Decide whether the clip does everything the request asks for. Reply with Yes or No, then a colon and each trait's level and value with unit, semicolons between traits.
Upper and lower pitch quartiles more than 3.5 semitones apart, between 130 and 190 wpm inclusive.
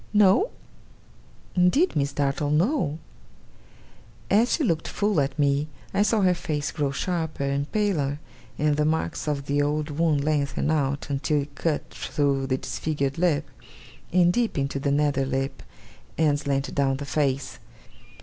No: average, 3.0 semitones; average, 150 wpm